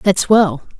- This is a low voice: No, medium, 185 Hz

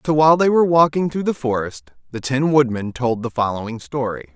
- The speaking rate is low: No, fast, 205 wpm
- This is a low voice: Yes, low, 130 Hz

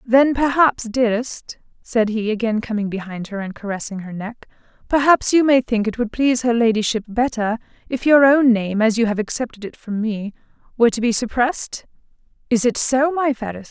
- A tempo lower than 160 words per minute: No, average, 180 wpm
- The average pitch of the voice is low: No, high, 235 Hz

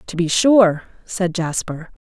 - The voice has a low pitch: No, medium, 180 Hz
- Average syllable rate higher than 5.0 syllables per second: No, 3.7 syllables/s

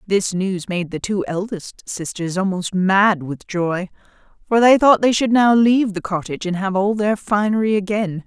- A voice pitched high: Yes, high, 195 Hz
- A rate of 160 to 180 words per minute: No, average, 190 wpm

